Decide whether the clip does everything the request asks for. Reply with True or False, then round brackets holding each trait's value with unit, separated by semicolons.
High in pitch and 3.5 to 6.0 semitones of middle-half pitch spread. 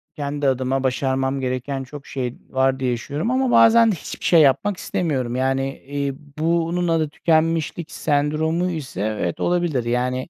False (140 Hz; 4.0 semitones)